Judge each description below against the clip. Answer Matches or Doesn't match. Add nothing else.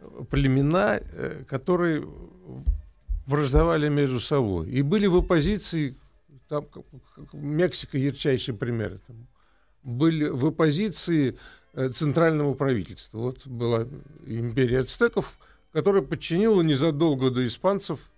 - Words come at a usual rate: Doesn't match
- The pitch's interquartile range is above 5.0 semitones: Doesn't match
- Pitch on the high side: Doesn't match